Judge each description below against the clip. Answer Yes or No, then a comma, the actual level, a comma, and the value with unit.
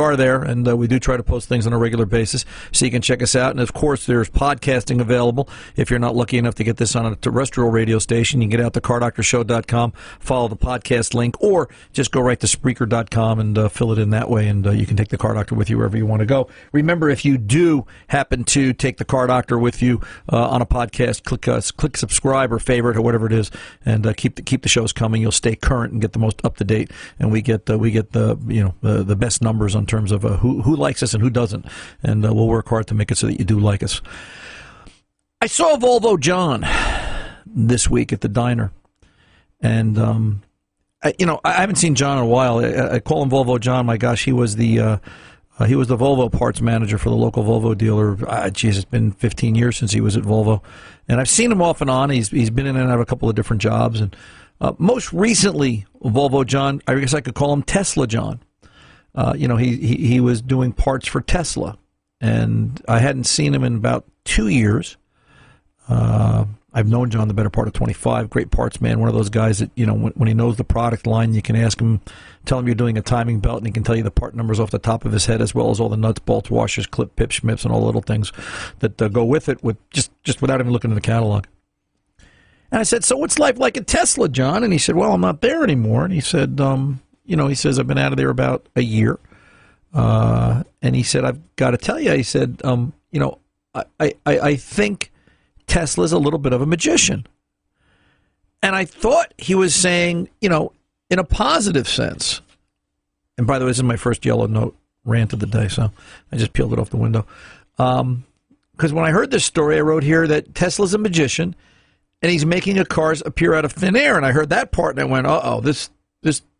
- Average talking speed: No, fast, 245 wpm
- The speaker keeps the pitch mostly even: No, average, 3.5 semitones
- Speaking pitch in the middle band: No, low, 120 Hz